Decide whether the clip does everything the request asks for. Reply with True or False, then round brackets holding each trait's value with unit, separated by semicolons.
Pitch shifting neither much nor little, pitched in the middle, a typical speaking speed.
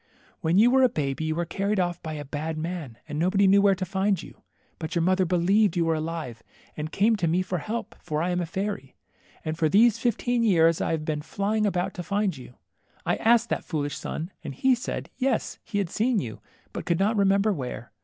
False (4.4 semitones; 180 Hz; 230 wpm)